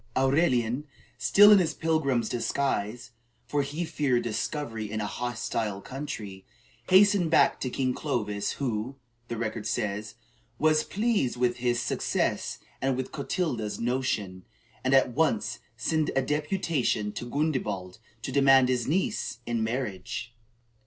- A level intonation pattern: No, average, 5.1 semitones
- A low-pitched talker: Yes, low, 125 Hz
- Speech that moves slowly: Yes, slow, 130 wpm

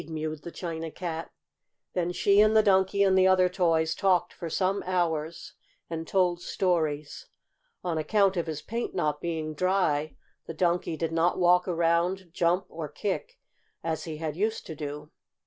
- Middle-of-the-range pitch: Yes, medium, 170 Hz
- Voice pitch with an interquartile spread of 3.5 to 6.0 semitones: No, average, 2.7 semitones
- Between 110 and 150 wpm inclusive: No, average, 165 wpm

